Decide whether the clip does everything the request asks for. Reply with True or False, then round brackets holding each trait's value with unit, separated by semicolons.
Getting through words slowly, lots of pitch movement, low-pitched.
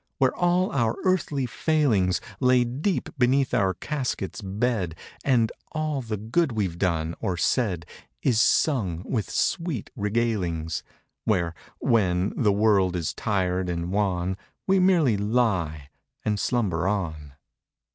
True (125 wpm; 5.8 semitones; 105 Hz)